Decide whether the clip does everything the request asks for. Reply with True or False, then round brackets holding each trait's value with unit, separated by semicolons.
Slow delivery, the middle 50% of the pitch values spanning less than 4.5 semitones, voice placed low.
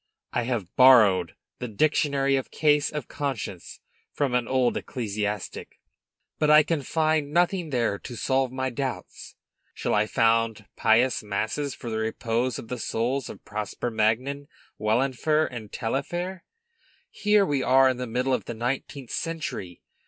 False (150 wpm; 4.1 semitones; 125 Hz)